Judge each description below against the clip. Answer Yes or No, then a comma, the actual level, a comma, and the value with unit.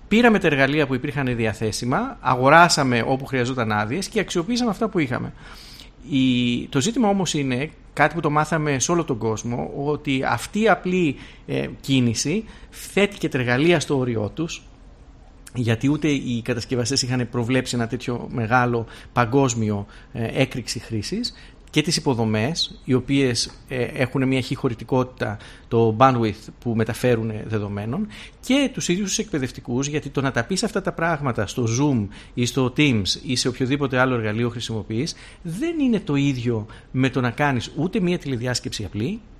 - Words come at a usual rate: Yes, average, 155 wpm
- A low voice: Yes, low, 130 Hz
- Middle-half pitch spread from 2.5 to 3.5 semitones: No, average, 4.3 semitones